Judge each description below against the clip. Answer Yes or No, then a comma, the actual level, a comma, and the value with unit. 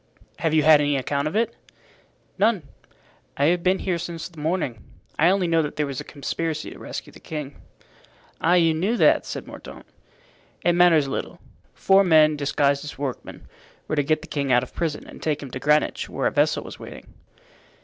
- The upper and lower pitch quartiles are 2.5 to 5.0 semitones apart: Yes, average, 3.1 semitones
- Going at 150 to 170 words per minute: No, average, 200 wpm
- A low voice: No, medium, 155 Hz